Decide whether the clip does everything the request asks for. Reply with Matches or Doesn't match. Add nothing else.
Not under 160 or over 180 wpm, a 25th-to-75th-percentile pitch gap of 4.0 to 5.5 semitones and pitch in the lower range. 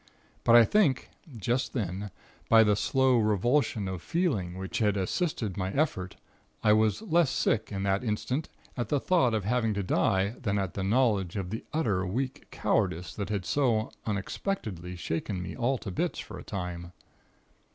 Matches